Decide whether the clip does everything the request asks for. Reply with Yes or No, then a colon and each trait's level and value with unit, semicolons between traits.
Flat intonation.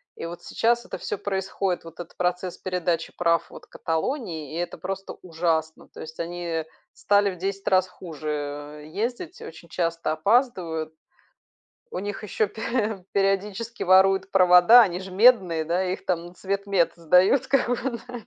No: average, 3.3 semitones